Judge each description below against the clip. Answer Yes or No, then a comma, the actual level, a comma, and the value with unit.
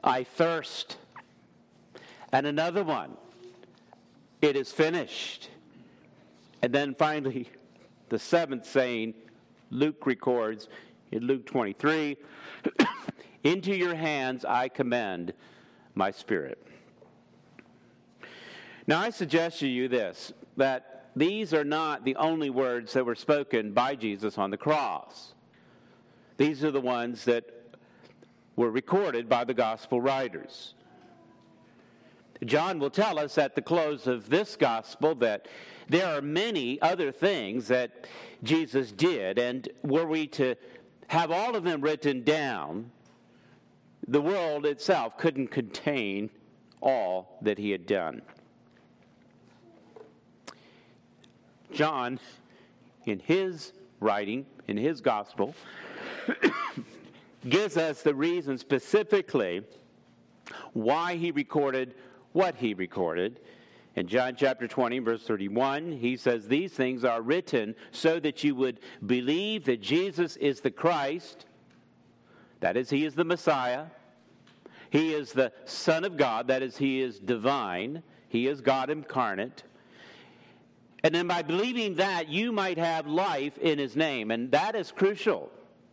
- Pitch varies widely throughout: No, average, 4.4 semitones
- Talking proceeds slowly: Yes, slow, 120 wpm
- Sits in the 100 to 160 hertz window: Yes, medium, 140 Hz